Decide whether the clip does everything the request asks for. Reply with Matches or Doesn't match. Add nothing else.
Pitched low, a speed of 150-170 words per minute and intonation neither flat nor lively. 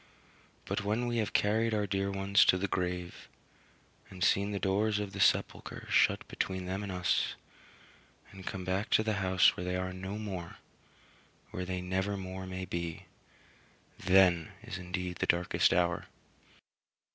Doesn't match